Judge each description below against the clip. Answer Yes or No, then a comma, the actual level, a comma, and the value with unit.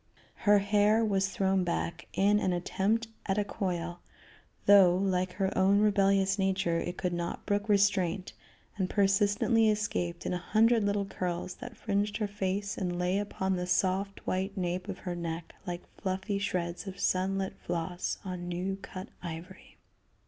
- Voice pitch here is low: No, high, 190 Hz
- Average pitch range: No, narrow, 2.2 semitones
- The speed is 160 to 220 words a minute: Yes, average, 165 wpm